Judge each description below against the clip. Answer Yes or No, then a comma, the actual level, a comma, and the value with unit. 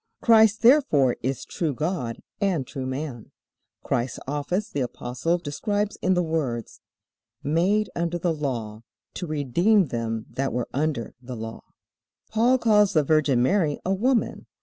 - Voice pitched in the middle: Yes, medium, 155 Hz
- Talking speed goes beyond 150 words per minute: No, average, 145 wpm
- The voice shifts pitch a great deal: Yes, wide, 7.2 semitones